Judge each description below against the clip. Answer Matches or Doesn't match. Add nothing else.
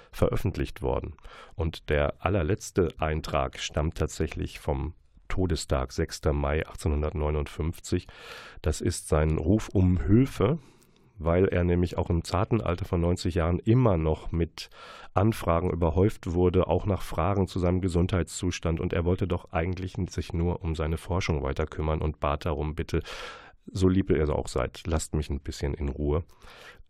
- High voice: Doesn't match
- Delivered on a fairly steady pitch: Doesn't match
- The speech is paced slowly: Doesn't match